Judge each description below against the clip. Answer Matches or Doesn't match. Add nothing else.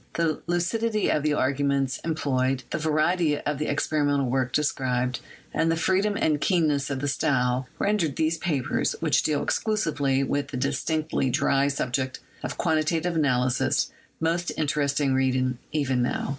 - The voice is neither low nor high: Matches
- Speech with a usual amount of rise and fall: Matches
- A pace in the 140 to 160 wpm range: Matches